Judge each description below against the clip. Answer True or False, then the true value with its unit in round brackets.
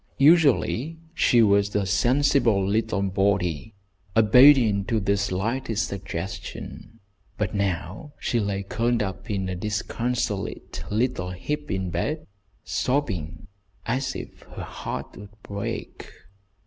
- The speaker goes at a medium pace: False (115 wpm)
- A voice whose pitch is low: True (105 Hz)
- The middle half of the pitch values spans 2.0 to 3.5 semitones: False (4.1 semitones)